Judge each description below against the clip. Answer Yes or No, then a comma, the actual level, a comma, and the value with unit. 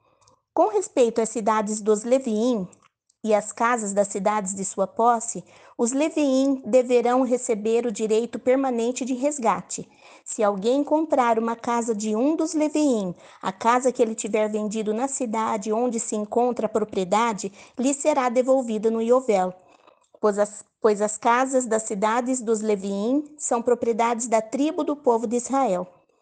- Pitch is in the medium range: No, high, 235 Hz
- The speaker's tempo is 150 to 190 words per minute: Yes, average, 155 wpm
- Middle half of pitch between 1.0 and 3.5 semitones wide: Yes, average, 3.1 semitones